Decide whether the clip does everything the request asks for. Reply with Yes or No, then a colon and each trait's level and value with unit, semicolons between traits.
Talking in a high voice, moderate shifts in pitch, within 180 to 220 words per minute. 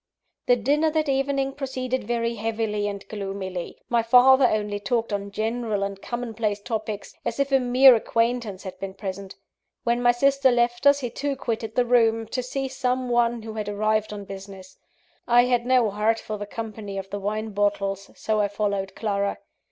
Yes: high, 225 Hz; average, 3.4 semitones; average, 185 wpm